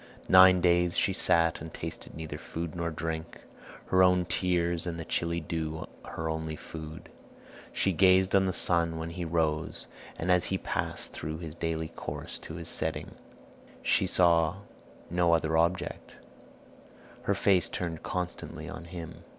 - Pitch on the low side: Yes, very low, 85 Hz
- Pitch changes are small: Yes, narrow, 1.8 semitones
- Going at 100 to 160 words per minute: Yes, average, 155 wpm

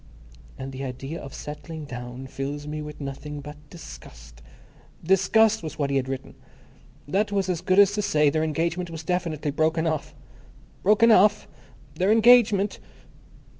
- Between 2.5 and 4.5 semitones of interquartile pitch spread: No, wide, 5.4 semitones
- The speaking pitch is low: No, medium, 155 Hz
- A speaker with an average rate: Yes, average, 165 wpm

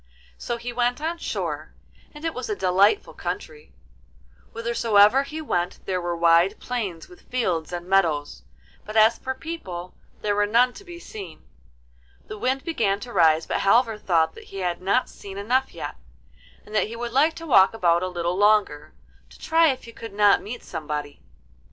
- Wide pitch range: Yes, wide, 5.8 semitones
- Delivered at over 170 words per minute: Yes, average, 180 wpm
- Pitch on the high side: Yes, high, 210 Hz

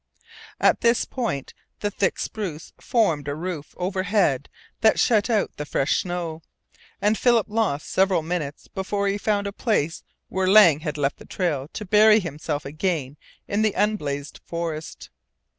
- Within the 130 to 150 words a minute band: No, average, 160 wpm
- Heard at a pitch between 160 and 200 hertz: Yes, medium, 185 Hz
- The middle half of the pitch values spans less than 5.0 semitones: No, wide, 5.5 semitones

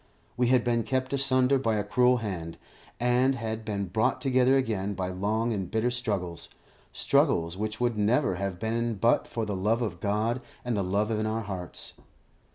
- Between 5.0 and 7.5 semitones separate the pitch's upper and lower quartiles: No, average, 3.5 semitones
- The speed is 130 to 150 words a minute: No, average, 180 wpm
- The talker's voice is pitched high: No, low, 110 Hz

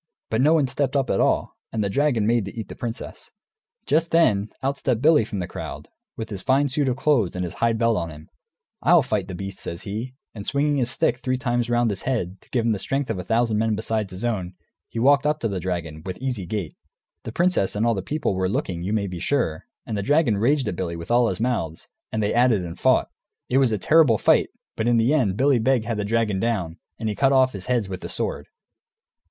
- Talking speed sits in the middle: No, fast, 250 wpm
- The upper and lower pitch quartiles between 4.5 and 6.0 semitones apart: Yes, average, 4.9 semitones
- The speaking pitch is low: Yes, low, 115 Hz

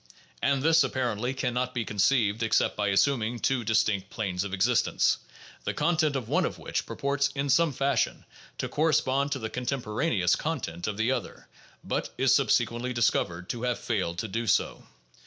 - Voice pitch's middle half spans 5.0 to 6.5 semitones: No, average, 4.4 semitones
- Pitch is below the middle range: Yes, low, 120 Hz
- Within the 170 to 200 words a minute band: Yes, average, 175 wpm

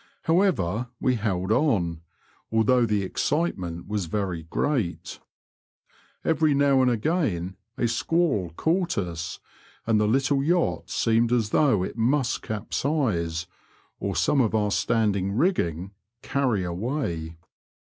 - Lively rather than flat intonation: Yes, wide, 7.1 semitones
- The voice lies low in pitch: Yes, low, 110 Hz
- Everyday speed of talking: No, slow, 120 wpm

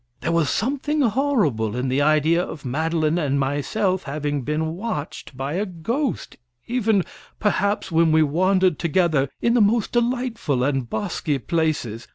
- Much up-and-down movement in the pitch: Yes, wide, 6.3 semitones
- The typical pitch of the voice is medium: Yes, medium, 165 Hz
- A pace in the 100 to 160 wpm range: Yes, average, 150 wpm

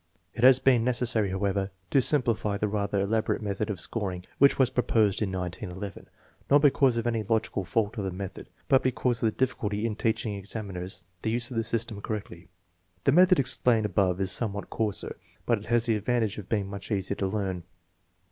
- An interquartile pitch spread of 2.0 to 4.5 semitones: Yes, average, 3.2 semitones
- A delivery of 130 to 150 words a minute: No, average, 190 wpm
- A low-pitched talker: Yes, low, 105 Hz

